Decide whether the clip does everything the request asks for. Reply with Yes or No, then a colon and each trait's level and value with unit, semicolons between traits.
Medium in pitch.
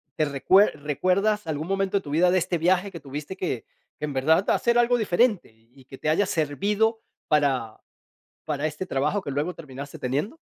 Yes: medium, 160 Hz